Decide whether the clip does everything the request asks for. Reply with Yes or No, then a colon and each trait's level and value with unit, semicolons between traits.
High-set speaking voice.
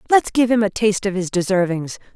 Yes: high, 205 Hz